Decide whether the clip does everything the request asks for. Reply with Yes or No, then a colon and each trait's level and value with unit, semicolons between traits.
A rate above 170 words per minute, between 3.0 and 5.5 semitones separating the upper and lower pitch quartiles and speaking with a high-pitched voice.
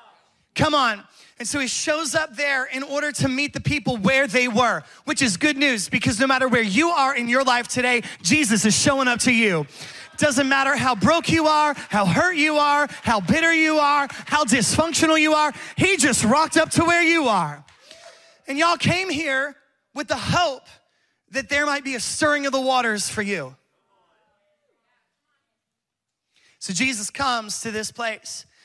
Yes: average, 180 wpm; average, 3.8 semitones; very high, 275 Hz